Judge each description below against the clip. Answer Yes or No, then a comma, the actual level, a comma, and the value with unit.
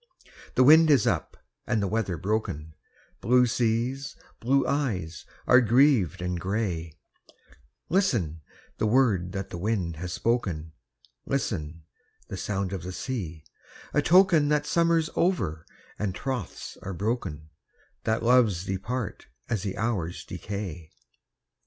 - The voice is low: Yes, low, 105 Hz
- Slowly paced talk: Yes, slow, 125 wpm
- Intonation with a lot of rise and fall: Yes, wide, 6.2 semitones